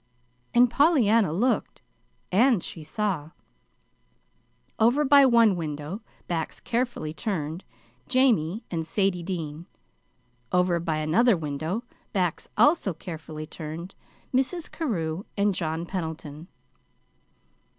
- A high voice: No, medium, 180 Hz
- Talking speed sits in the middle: No, slow, 100 wpm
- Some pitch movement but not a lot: No, wide, 6.6 semitones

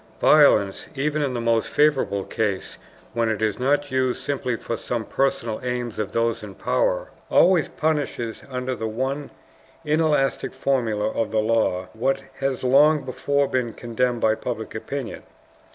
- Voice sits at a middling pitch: No, low, 125 Hz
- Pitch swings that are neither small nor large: Yes, average, 3.8 semitones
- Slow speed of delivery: No, average, 150 wpm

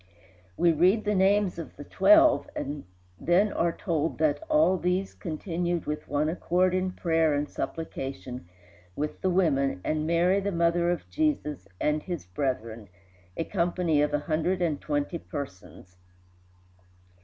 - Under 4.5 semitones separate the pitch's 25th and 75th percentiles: Yes, average, 3.7 semitones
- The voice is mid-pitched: Yes, medium, 165 Hz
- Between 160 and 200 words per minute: No, average, 145 wpm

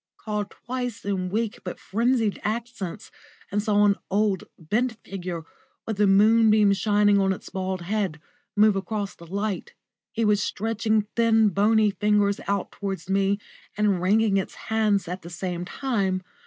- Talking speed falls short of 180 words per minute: Yes, average, 155 wpm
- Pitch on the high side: Yes, high, 205 Hz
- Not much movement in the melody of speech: Yes, narrow, 2.1 semitones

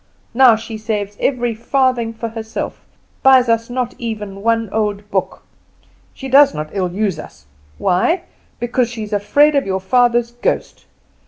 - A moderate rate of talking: Yes, average, 155 wpm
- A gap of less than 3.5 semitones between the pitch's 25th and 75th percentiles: Yes, average, 3.0 semitones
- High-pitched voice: Yes, high, 230 Hz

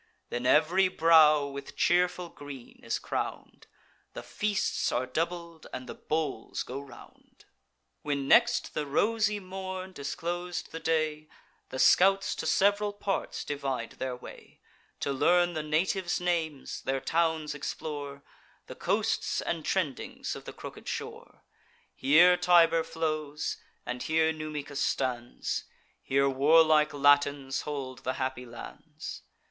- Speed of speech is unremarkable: No, slow, 130 wpm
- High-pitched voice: No, medium, 155 Hz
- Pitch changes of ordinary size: Yes, average, 4.0 semitones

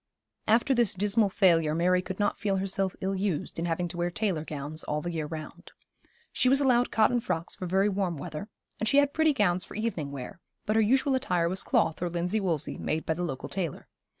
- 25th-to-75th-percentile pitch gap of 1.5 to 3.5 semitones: No, average, 4.3 semitones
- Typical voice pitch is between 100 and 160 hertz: No, medium, 185 Hz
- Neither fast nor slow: No, fast, 220 wpm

